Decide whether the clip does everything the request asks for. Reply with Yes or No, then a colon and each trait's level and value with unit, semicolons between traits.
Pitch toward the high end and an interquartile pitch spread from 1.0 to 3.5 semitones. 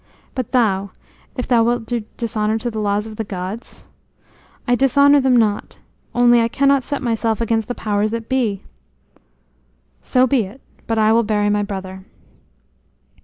Yes: high, 225 Hz; average, 2.7 semitones